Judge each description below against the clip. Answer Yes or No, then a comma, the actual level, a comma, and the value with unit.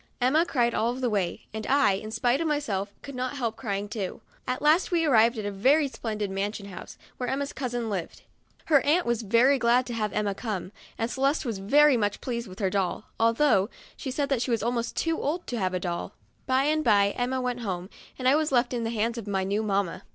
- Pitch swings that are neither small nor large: Yes, average, 4.6 semitones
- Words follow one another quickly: Yes, fast, 230 wpm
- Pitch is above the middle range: Yes, high, 235 Hz